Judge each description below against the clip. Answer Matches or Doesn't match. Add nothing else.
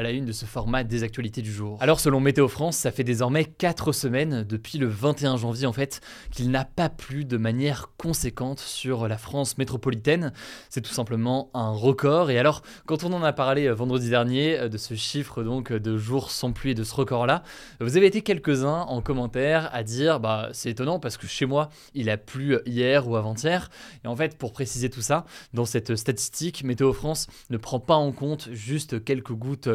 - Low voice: Matches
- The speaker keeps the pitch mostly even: Doesn't match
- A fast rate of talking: Doesn't match